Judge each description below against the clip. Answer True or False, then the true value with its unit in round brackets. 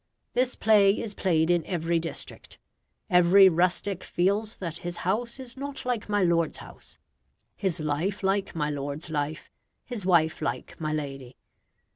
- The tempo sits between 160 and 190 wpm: False (150 wpm)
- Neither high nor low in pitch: True (180 Hz)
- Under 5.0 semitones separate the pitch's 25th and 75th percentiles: True (4.3 semitones)